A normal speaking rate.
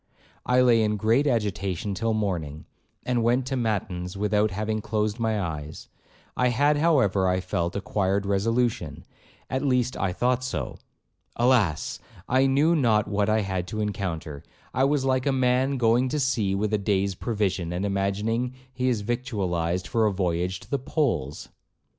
Yes: average, 160 wpm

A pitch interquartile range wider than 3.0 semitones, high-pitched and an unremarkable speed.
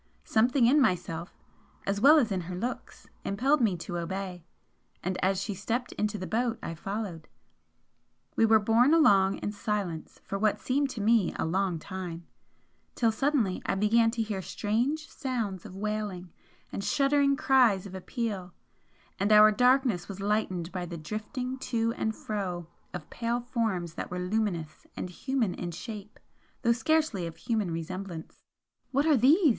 Yes: average, 4.7 semitones; high, 210 Hz; average, 160 wpm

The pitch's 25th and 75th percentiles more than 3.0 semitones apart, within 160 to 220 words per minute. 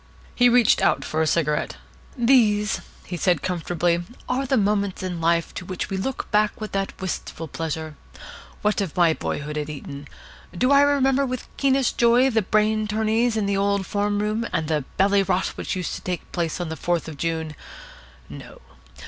Yes: average, 4.9 semitones; average, 190 wpm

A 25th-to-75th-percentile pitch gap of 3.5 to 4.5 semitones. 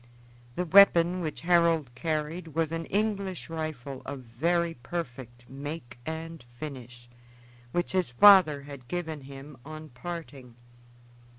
Yes: average, 4.2 semitones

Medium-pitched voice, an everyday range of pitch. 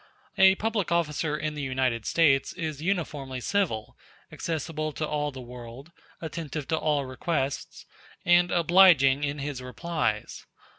Yes: medium, 150 Hz; average, 4.1 semitones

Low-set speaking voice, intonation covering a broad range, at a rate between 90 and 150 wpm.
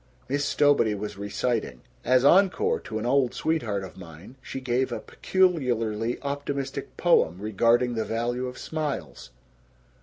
No: low, 125 Hz; average, 4.7 semitones; average, 140 wpm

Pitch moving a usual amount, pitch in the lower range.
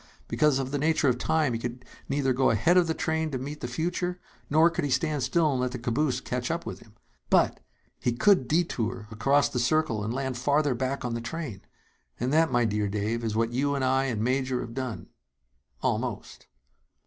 Yes: average, 4.0 semitones; low, 130 Hz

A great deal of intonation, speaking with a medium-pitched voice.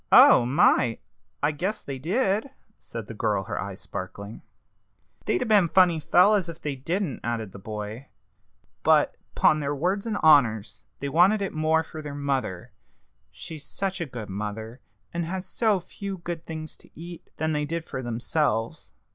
Yes: wide, 7.2 semitones; medium, 150 Hz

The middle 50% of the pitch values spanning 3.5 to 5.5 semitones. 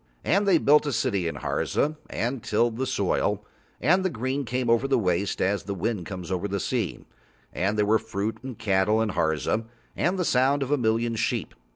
Yes: average, 4.8 semitones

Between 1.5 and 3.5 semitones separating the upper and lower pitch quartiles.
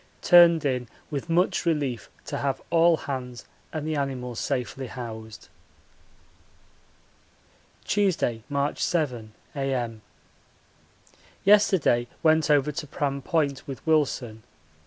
No: average, 4.2 semitones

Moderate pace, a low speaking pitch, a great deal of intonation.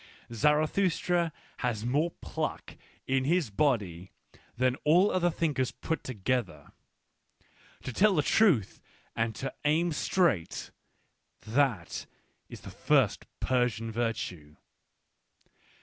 No: slow, 100 wpm; low, 130 Hz; wide, 6.2 semitones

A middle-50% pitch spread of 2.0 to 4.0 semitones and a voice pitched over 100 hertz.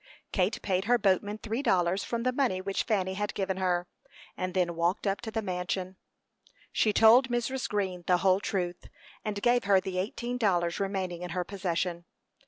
Yes: average, 3.2 semitones; high, 190 Hz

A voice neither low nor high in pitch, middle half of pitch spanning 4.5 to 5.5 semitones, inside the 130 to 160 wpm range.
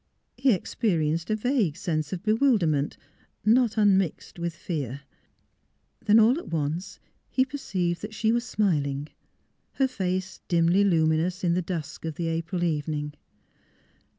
Yes: medium, 180 Hz; average, 5.2 semitones; average, 145 wpm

